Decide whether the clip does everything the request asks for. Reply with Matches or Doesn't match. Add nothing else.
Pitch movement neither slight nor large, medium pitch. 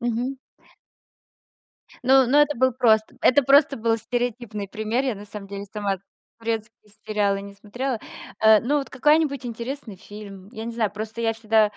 Doesn't match